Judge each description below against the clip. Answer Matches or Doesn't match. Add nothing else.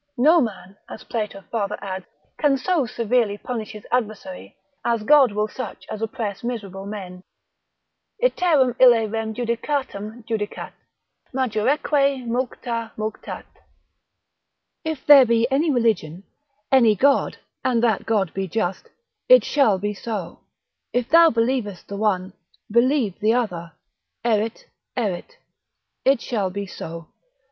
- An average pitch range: Matches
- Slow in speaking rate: Matches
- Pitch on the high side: Matches